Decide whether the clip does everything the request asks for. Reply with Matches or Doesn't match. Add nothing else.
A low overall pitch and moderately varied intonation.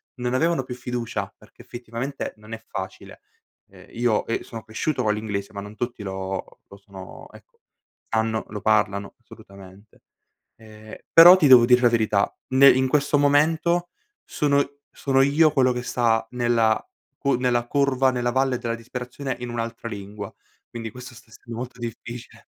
Matches